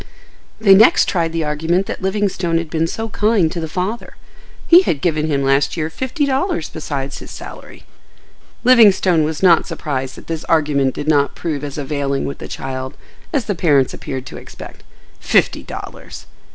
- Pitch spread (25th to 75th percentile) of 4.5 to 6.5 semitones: Yes, average, 5.1 semitones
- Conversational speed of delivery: Yes, average, 170 wpm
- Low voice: No, medium, 160 Hz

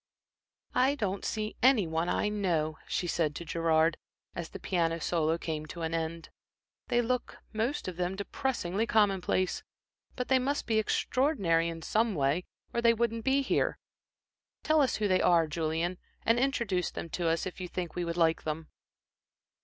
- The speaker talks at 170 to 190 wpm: Yes, average, 175 wpm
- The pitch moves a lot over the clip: Yes, wide, 5.7 semitones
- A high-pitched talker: No, medium, 180 Hz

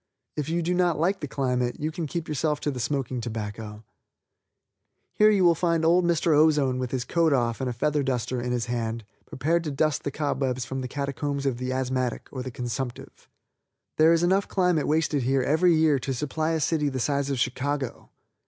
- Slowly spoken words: No, fast, 205 wpm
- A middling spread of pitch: Yes, average, 4.0 semitones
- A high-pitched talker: No, medium, 140 Hz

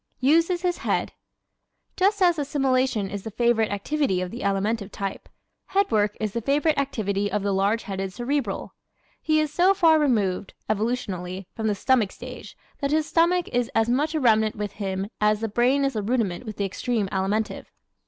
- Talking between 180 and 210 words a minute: Yes, average, 185 wpm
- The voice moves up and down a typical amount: No, wide, 5.9 semitones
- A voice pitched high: Yes, high, 225 Hz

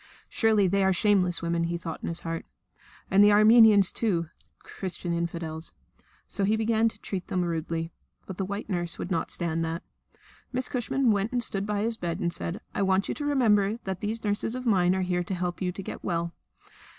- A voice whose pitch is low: No, high, 190 Hz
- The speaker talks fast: Yes, fast, 210 wpm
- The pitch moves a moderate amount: Yes, average, 3.7 semitones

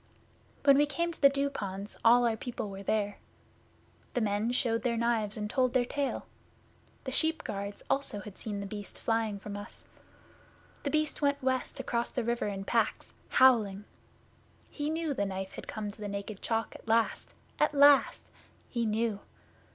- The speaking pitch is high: Yes, high, 230 Hz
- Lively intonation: No, average, 4.6 semitones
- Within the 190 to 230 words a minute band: No, average, 175 wpm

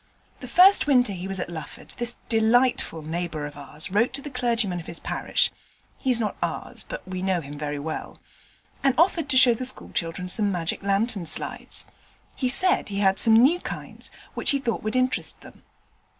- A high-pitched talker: Yes, high, 210 Hz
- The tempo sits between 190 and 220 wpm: Yes, average, 195 wpm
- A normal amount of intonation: No, wide, 6.5 semitones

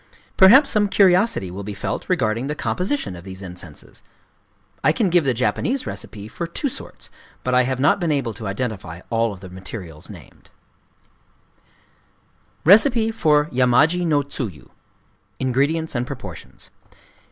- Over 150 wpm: No, average, 140 wpm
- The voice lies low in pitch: Yes, low, 130 Hz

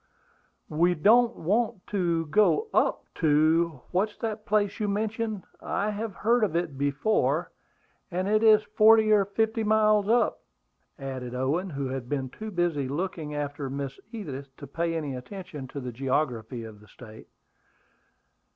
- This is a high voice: No, medium, 175 Hz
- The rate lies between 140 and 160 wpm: Yes, average, 150 wpm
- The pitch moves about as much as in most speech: No, wide, 7.3 semitones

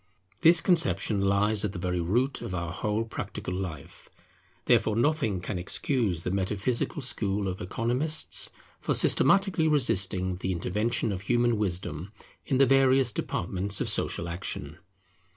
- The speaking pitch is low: Yes, low, 105 Hz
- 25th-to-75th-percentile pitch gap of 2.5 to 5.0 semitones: No, wide, 5.6 semitones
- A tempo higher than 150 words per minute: No, average, 140 wpm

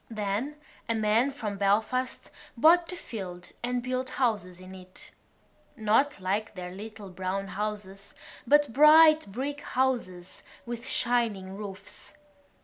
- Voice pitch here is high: Yes, high, 215 Hz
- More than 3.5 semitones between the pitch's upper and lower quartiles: Yes, average, 4.8 semitones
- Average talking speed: No, slow, 120 wpm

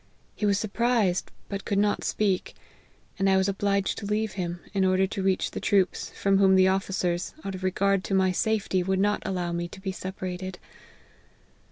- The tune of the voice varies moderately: No, narrow, 1.2 semitones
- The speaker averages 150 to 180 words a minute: No, average, 195 wpm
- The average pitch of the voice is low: No, high, 190 Hz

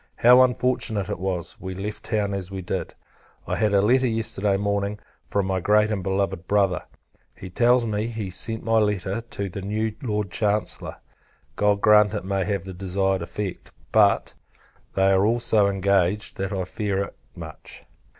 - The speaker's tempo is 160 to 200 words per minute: Yes, average, 180 wpm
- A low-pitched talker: Yes, low, 100 Hz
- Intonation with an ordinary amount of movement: No, narrow, 1.9 semitones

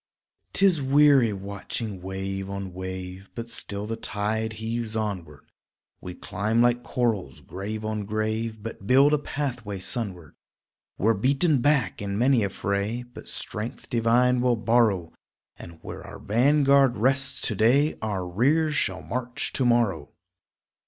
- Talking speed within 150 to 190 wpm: No, average, 140 wpm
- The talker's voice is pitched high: No, low, 110 Hz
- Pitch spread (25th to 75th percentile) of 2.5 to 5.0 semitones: Yes, average, 4.0 semitones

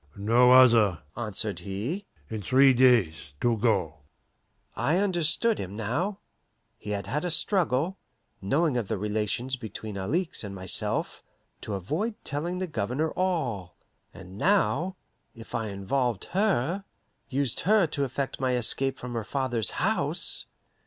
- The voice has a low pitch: Yes, low, 125 Hz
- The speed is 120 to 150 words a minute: Yes, average, 140 wpm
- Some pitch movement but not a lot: No, wide, 7.4 semitones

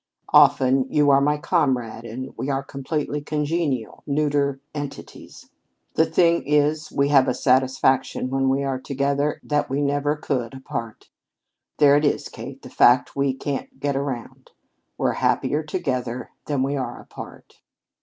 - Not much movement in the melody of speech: Yes, narrow, 1.9 semitones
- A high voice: No, medium, 140 Hz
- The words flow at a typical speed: Yes, average, 150 wpm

